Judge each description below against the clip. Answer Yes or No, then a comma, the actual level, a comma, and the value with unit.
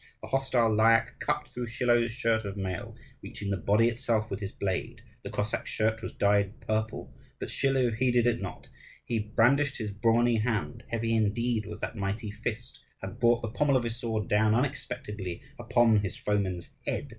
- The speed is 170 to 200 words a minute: Yes, average, 180 wpm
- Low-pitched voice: Yes, low, 115 Hz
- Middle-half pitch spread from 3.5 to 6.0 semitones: No, narrow, 2.4 semitones